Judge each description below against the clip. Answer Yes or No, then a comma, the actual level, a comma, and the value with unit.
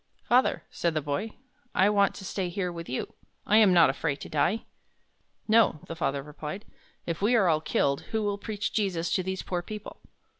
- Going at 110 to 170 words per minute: No, average, 195 wpm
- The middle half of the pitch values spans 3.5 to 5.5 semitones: Yes, average, 4.5 semitones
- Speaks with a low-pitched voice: No, medium, 185 Hz